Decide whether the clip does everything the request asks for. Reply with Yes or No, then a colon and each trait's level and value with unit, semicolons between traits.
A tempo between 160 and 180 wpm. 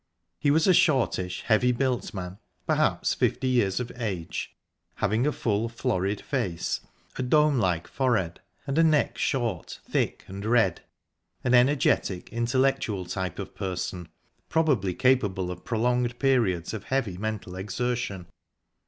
No: slow, 135 wpm